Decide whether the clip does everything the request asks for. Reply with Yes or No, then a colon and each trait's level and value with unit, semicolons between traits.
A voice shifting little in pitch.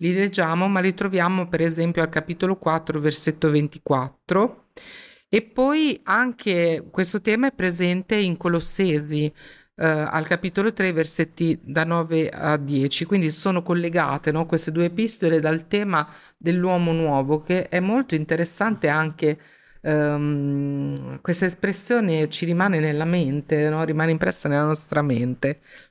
No: average, 3.4 semitones